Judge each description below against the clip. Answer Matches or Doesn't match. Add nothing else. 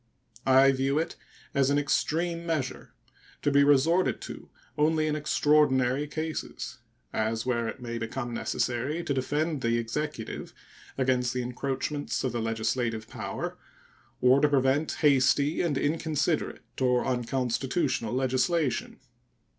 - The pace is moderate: Doesn't match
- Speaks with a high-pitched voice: Doesn't match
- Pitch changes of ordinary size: Matches